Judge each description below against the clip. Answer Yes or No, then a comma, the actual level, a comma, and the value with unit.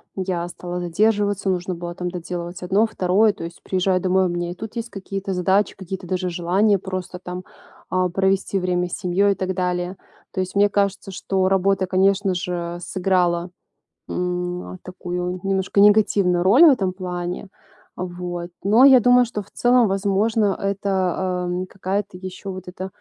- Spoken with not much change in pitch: Yes, narrow, 1.8 semitones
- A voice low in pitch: No, medium, 185 Hz